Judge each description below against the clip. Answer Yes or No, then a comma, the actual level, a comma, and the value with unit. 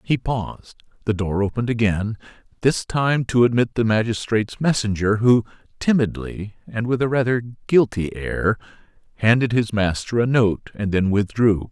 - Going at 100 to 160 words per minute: Yes, average, 150 wpm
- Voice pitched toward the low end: Yes, low, 110 Hz